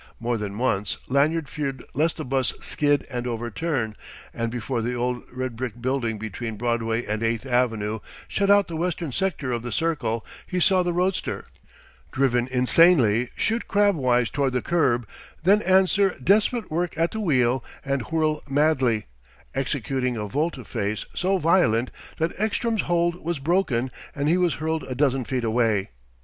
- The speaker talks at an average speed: Yes, average, 160 wpm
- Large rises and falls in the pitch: Yes, wide, 5.9 semitones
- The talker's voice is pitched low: Yes, low, 130 Hz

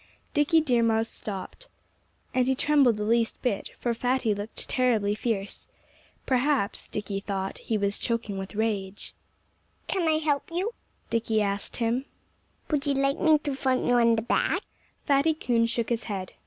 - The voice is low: No, high, 235 Hz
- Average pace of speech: Yes, average, 165 wpm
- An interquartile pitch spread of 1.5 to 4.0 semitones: No, average, 4.6 semitones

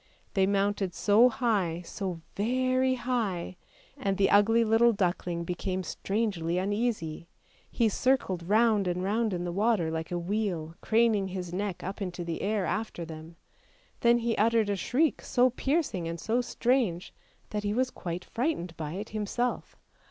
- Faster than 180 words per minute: No, average, 160 wpm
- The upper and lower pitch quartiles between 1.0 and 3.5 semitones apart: No, average, 4.7 semitones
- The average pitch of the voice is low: No, high, 205 Hz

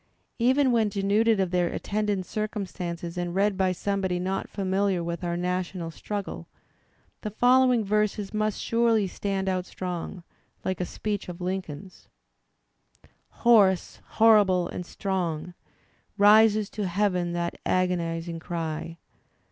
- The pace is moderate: No, slow, 130 wpm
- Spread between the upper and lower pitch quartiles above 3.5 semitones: No, average, 3.0 semitones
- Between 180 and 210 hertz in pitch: Yes, high, 190 Hz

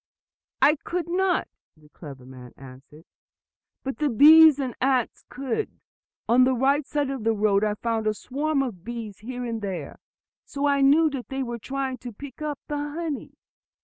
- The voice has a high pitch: Yes, very high, 260 Hz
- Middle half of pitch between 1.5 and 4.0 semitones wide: No, average, 5.1 semitones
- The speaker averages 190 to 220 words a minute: No, average, 180 wpm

